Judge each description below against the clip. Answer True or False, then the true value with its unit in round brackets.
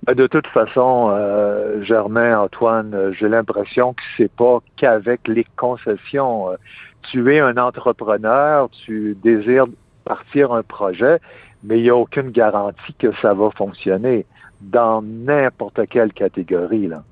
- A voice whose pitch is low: True (115 Hz)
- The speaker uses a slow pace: True (135 wpm)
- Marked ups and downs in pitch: False (3.0 semitones)